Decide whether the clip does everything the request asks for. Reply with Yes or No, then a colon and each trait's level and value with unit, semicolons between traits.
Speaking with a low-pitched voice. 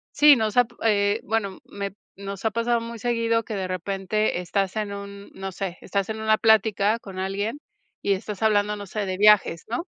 No: high, 205 Hz